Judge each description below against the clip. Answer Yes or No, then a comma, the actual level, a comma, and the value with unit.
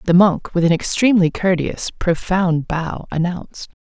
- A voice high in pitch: No, medium, 175 Hz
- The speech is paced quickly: No, average, 140 wpm